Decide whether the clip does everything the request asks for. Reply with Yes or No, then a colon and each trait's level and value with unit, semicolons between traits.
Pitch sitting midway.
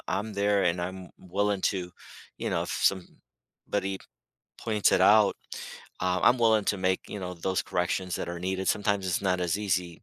No: very low, 95 Hz